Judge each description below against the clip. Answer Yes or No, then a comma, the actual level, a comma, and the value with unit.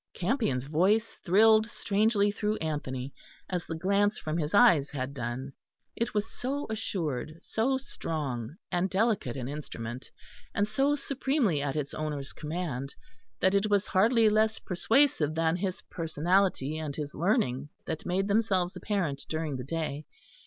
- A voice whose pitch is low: No, medium, 175 Hz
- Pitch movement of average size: No, wide, 6.4 semitones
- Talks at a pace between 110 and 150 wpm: Yes, average, 145 wpm